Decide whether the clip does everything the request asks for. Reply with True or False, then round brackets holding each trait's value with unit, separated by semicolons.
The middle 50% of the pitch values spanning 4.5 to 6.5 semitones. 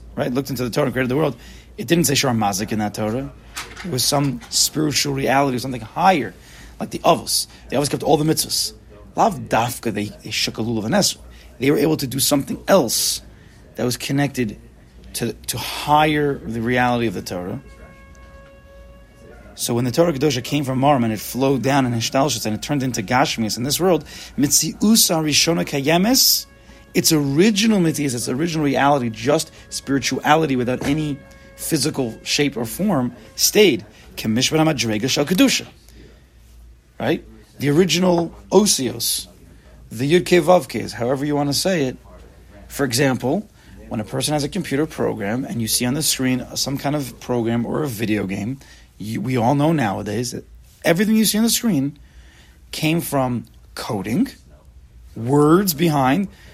True (5.3 semitones)